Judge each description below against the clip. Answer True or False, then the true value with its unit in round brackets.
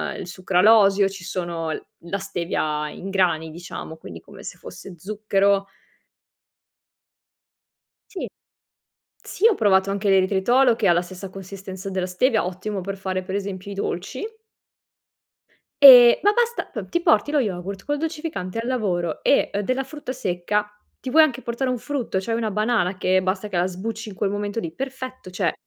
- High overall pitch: True (195 Hz)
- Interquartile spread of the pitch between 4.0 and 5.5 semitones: True (4.5 semitones)